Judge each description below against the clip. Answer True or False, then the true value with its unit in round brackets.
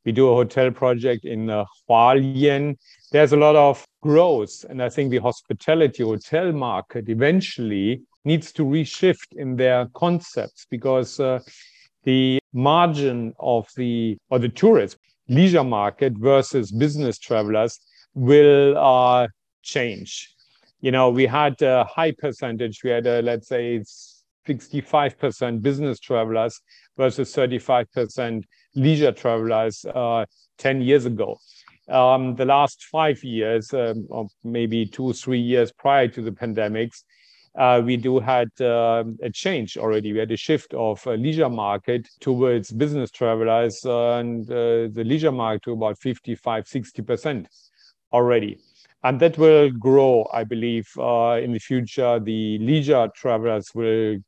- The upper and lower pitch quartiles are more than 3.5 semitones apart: False (3.2 semitones)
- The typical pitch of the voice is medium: False (125 Hz)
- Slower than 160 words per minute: True (145 wpm)